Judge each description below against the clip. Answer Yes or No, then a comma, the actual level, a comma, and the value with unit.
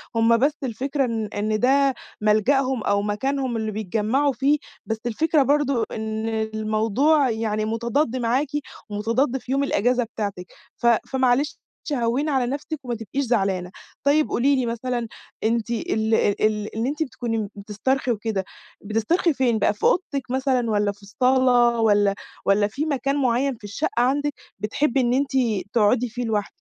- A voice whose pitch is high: Yes, high, 235 Hz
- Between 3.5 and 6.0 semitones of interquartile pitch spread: Yes, average, 3.8 semitones